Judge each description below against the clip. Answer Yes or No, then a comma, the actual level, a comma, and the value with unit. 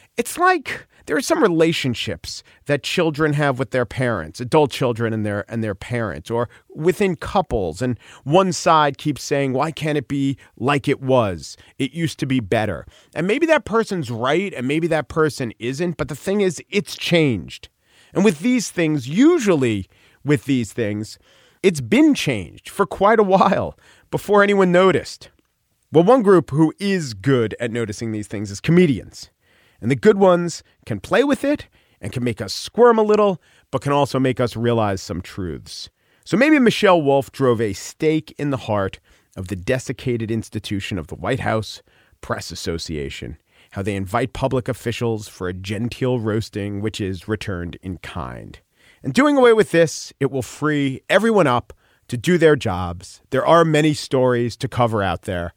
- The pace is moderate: Yes, average, 175 wpm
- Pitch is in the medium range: No, low, 130 Hz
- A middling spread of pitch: No, wide, 7.4 semitones